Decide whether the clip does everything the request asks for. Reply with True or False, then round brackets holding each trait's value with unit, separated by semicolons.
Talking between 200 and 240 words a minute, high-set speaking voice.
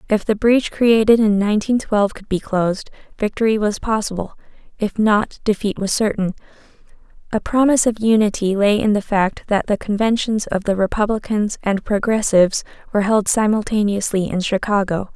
False (155 wpm; 210 Hz)